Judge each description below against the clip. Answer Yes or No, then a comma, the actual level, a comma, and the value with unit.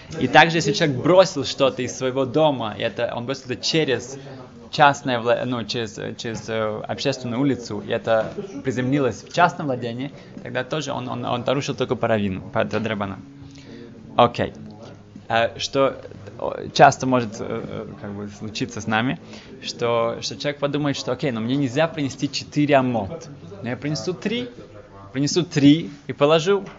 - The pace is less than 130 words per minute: No, average, 150 wpm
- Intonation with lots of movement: No, average, 4.0 semitones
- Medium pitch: No, low, 130 Hz